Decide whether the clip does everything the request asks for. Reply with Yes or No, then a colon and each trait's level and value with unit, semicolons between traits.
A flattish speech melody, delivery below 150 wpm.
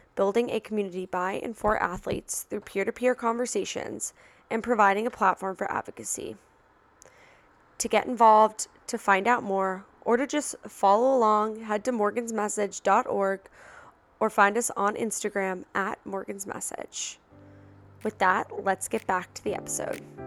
No: average, 3.1 semitones; average, 140 wpm